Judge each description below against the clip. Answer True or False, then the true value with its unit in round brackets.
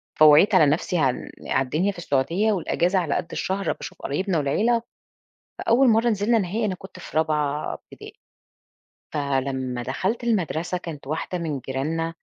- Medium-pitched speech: True (165 Hz)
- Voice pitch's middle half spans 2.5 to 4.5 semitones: False (5.5 semitones)